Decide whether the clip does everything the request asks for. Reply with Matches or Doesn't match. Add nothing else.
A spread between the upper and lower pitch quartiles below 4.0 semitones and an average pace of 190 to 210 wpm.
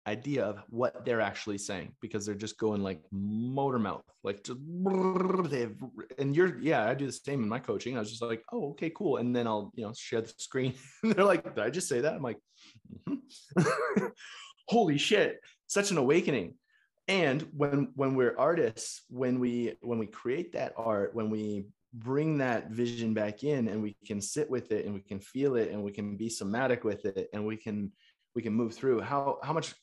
Doesn't match